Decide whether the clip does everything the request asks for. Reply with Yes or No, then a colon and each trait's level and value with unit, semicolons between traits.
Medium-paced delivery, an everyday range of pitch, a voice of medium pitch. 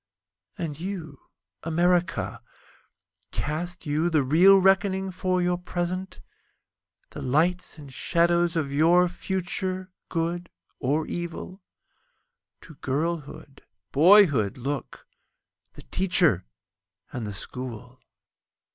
No: slow, 80 wpm; average, 3.8 semitones; medium, 170 Hz